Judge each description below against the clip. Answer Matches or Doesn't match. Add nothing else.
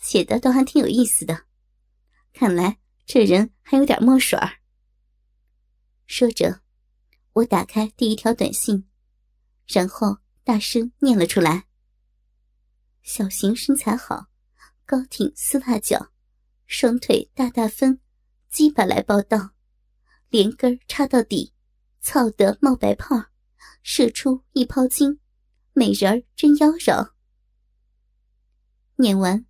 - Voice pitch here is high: Matches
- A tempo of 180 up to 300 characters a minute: Doesn't match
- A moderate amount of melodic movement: Matches